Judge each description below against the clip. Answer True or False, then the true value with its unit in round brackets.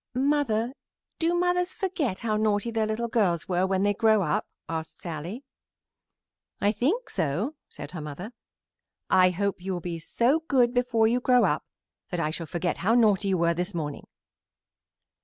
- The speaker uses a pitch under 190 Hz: False (210 Hz)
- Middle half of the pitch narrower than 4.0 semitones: False (5.6 semitones)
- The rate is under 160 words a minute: False (170 wpm)